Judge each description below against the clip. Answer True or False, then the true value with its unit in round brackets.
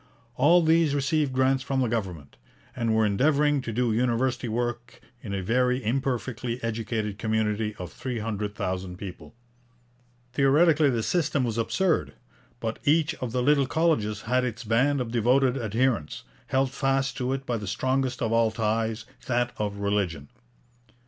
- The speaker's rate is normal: True (155 wpm)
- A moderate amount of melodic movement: True (3.6 semitones)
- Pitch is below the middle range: True (120 Hz)